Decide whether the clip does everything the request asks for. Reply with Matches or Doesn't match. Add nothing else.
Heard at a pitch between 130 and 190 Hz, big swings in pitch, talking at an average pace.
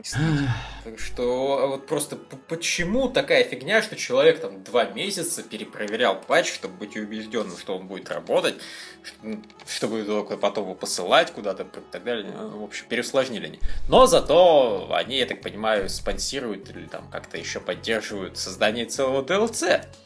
Matches